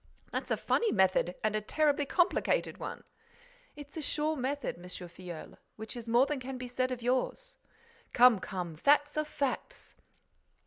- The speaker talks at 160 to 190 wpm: Yes, average, 165 wpm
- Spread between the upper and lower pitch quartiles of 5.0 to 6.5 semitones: Yes, wide, 5.6 semitones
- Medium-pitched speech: No, very high, 255 Hz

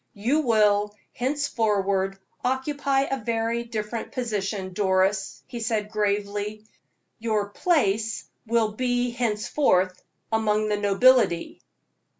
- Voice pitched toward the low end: No, high, 215 Hz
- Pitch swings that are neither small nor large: Yes, average, 3.1 semitones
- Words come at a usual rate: No, slow, 100 wpm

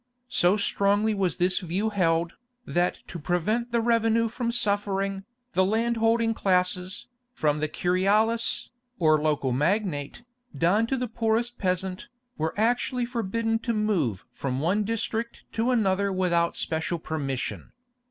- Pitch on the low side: No, high, 200 Hz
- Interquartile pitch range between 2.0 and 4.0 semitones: No, average, 4.5 semitones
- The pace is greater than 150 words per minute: No, slow, 135 wpm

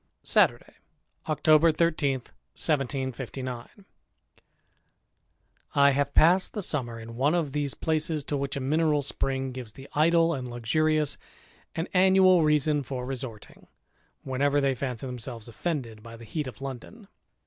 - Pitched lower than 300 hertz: Yes, medium, 140 Hz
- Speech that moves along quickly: No, slow, 135 wpm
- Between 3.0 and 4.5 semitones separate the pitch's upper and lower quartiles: Yes, average, 3.5 semitones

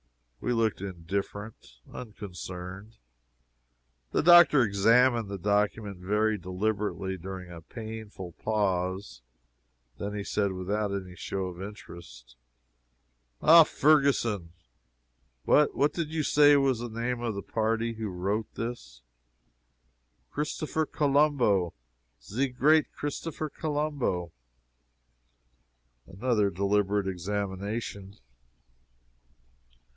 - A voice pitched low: Yes, low, 105 Hz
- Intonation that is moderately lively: Yes, average, 4.4 semitones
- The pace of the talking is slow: Yes, slow, 95 wpm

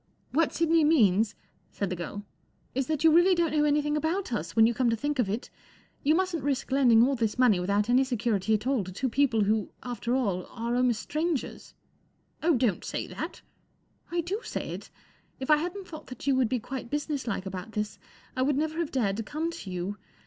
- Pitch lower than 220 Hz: No, very high, 255 Hz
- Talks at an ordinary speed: No, fast, 230 wpm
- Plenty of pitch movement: Yes, wide, 5.8 semitones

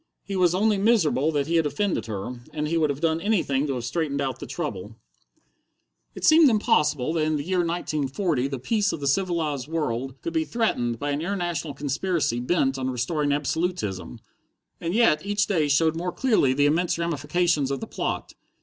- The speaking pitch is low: No, medium, 155 Hz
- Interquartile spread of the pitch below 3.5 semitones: No, average, 4.3 semitones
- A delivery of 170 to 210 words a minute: Yes, average, 190 wpm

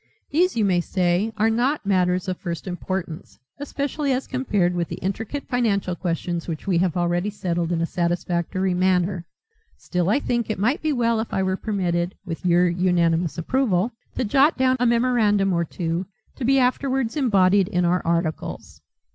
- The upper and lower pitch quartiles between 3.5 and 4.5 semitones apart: No, average, 5.2 semitones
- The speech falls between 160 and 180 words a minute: Yes, average, 175 wpm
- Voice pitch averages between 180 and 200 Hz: Yes, high, 190 Hz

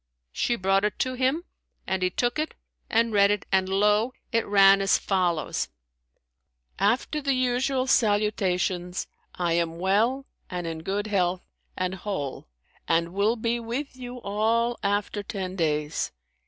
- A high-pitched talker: Yes, high, 205 Hz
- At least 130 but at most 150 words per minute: Yes, average, 145 wpm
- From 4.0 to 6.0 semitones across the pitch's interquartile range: Yes, average, 4.3 semitones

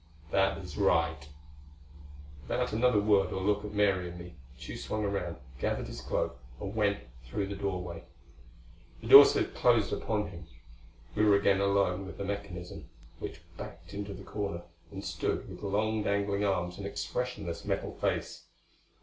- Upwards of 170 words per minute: No, average, 160 wpm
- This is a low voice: Yes, low, 100 Hz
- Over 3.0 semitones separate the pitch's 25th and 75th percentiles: No, narrow, 2.5 semitones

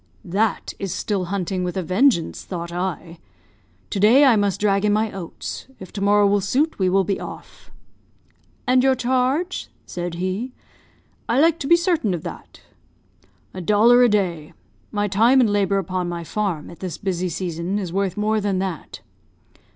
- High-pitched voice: Yes, high, 200 Hz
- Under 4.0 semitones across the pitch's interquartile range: Yes, average, 3.5 semitones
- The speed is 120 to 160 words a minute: No, average, 175 wpm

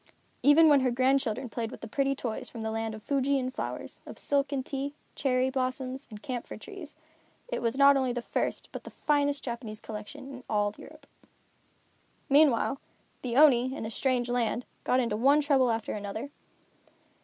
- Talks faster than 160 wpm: Yes, average, 180 wpm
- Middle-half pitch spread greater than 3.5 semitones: No, average, 3.2 semitones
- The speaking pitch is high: Yes, very high, 255 Hz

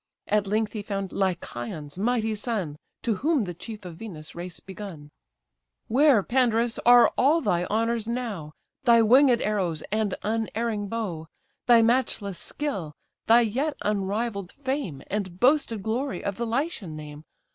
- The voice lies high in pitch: Yes, high, 215 Hz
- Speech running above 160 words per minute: No, average, 145 wpm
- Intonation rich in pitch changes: No, average, 4.2 semitones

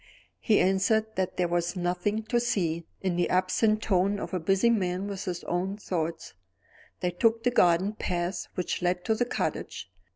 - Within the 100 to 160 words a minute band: No, average, 175 wpm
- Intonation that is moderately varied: Yes, average, 3.3 semitones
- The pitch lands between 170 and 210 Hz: Yes, medium, 185 Hz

